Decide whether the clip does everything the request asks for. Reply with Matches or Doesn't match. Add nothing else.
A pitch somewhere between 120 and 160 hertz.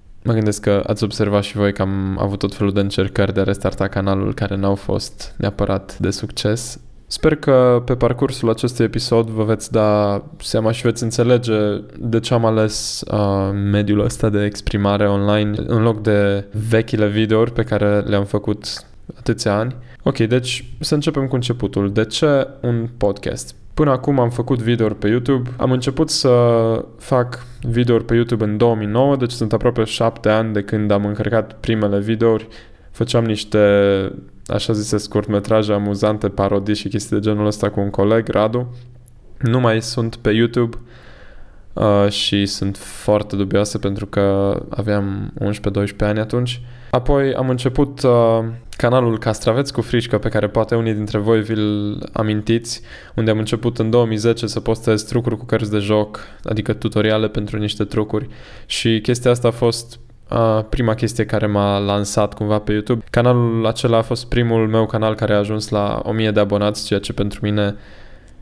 Doesn't match